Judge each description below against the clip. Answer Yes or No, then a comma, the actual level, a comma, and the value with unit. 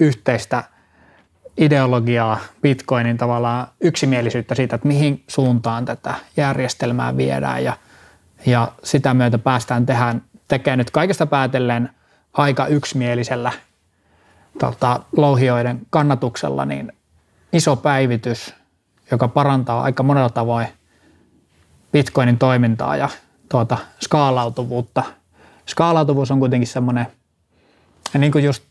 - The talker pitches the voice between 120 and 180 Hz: Yes, low, 125 Hz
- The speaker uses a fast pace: No, slow, 95 wpm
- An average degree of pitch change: Yes, average, 3.1 semitones